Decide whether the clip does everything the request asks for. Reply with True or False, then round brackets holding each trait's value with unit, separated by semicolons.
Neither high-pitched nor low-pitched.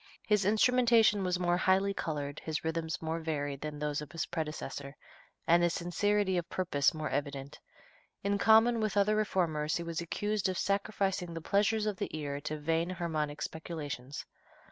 True (170 Hz)